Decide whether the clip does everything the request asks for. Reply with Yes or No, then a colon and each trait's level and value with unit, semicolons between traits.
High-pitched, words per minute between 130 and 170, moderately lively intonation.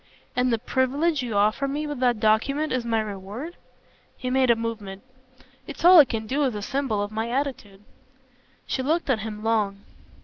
No: high, 240 Hz; average, 190 wpm; average, 4.3 semitones